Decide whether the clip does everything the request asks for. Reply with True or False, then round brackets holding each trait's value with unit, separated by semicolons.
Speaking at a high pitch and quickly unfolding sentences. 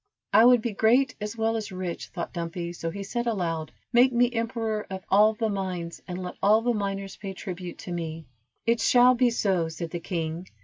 True (200 Hz; 210 wpm)